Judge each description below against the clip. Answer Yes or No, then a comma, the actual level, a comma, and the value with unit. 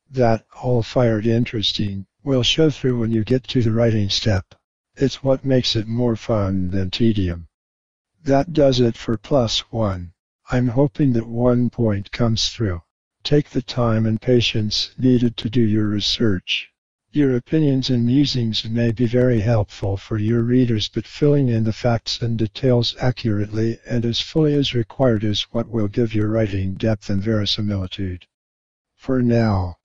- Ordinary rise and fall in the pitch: Yes, average, 3.2 semitones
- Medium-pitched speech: No, low, 115 Hz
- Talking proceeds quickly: No, average, 160 wpm